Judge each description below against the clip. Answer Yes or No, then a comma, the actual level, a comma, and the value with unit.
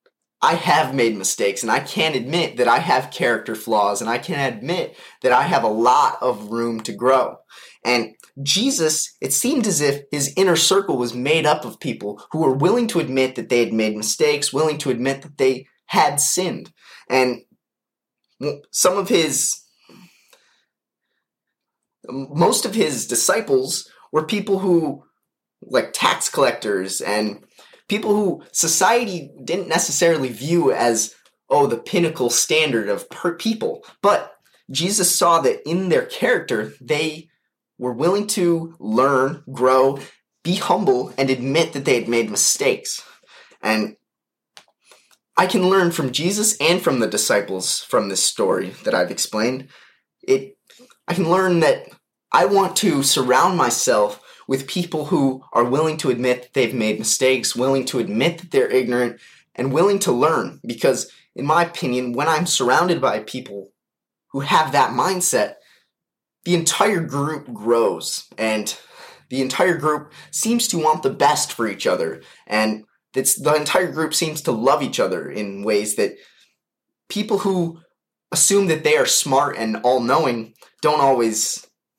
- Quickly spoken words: No, average, 150 wpm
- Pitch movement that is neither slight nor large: No, wide, 6.3 semitones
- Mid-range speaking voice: Yes, medium, 155 Hz